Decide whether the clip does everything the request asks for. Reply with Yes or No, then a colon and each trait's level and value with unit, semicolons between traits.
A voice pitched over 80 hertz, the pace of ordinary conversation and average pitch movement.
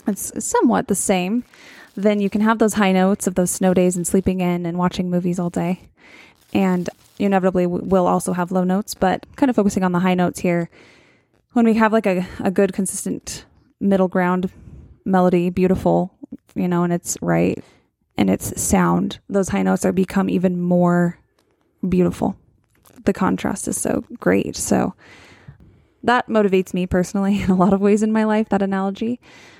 No: high, 190 Hz; average, 175 wpm; narrow, 2.3 semitones